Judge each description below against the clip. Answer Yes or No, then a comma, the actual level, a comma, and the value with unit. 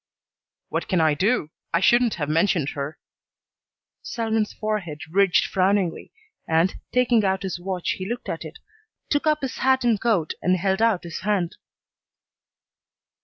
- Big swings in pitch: No, average, 4.7 semitones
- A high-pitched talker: Yes, high, 195 Hz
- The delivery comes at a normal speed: Yes, average, 150 wpm